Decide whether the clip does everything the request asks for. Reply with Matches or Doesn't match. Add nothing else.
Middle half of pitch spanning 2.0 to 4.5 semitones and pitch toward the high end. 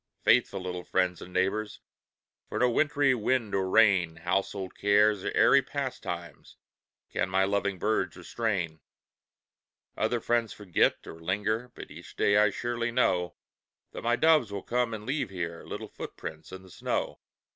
Doesn't match